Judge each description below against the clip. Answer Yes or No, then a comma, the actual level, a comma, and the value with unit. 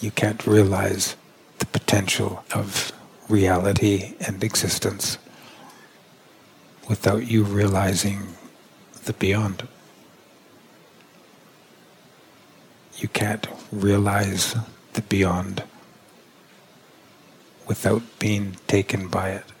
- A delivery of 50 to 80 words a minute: Yes, slow, 75 wpm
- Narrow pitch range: Yes, narrow, 1.8 semitones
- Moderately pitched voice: No, low, 100 Hz